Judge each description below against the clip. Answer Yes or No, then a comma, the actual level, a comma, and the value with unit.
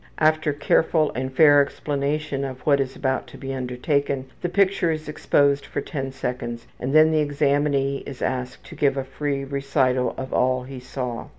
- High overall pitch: No, medium, 140 Hz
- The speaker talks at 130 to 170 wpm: No, average, 180 wpm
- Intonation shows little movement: Yes, narrow, 2.2 semitones